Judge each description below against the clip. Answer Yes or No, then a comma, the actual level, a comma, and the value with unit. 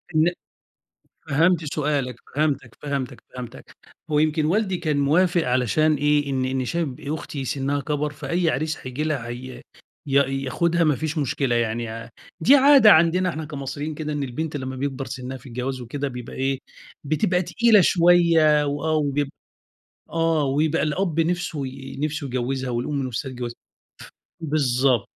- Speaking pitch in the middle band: Yes, medium, 145 Hz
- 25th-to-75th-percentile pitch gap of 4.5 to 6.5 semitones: No, average, 3.3 semitones